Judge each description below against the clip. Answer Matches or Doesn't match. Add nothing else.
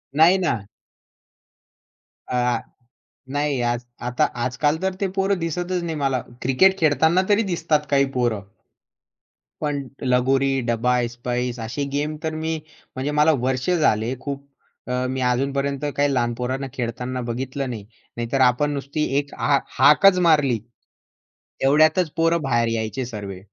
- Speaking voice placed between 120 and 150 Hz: Matches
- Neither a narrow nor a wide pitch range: Matches